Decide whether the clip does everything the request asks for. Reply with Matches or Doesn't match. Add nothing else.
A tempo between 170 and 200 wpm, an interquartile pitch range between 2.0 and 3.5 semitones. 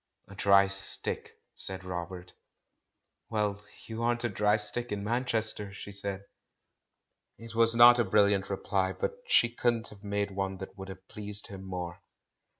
Doesn't match